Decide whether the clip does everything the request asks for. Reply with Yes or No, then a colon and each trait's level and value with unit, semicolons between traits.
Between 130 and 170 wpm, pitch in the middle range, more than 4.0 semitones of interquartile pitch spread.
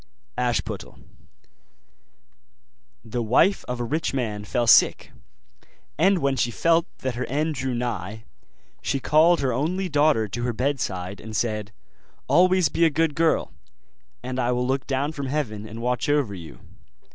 No: average, 155 wpm; low, 130 Hz; average, 4.7 semitones